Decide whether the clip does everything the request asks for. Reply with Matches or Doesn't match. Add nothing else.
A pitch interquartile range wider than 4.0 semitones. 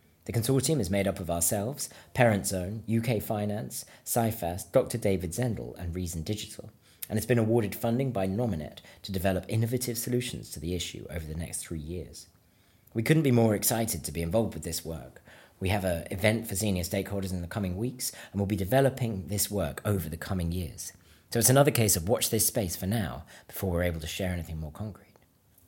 Matches